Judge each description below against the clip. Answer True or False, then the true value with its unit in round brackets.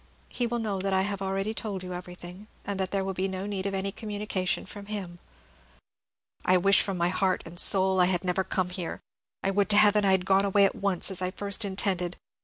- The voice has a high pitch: True (195 Hz)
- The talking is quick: True (230 wpm)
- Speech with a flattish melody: True (1.5 semitones)